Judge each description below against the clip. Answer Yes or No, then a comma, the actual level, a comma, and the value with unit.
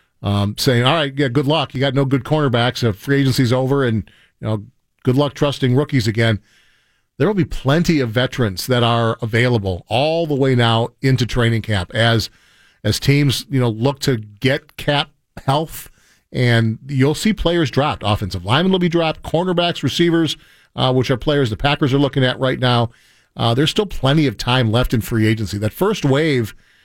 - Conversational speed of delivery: Yes, average, 190 wpm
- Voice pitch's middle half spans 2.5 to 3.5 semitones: No, average, 3.9 semitones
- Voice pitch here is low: Yes, low, 130 Hz